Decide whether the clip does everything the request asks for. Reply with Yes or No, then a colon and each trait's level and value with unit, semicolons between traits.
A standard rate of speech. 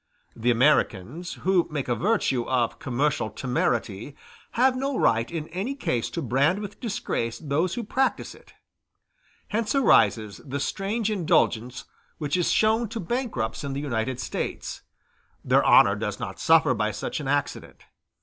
Yes: average, 150 wpm